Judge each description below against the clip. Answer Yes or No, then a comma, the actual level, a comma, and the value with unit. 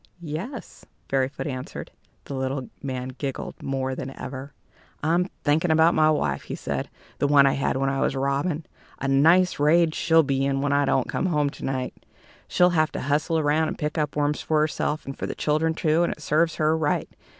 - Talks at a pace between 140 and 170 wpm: No, fast, 205 wpm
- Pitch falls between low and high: Yes, medium, 150 Hz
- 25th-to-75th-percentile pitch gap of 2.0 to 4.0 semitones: Yes, average, 2.7 semitones